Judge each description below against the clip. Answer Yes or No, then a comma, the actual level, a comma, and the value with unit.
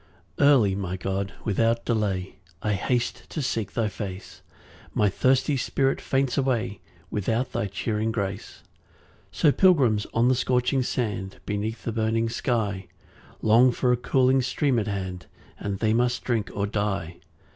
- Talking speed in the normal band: Yes, average, 155 wpm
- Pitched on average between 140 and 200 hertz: No, low, 110 Hz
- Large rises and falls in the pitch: No, average, 3.7 semitones